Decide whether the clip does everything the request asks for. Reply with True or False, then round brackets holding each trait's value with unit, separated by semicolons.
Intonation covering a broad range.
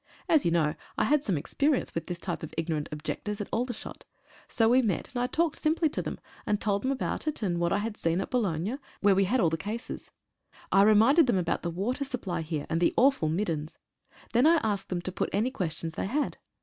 True (6.7 semitones)